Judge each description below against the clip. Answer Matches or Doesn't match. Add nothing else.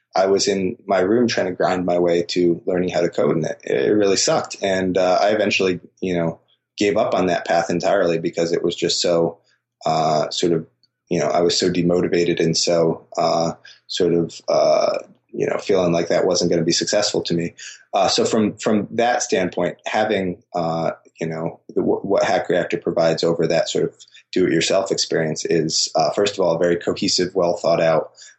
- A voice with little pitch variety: Matches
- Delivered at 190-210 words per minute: Matches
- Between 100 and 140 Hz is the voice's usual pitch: Doesn't match